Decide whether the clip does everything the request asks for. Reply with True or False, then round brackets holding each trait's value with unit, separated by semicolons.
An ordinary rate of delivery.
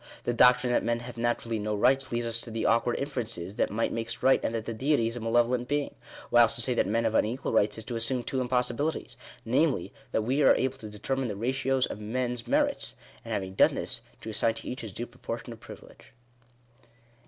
False (220 wpm)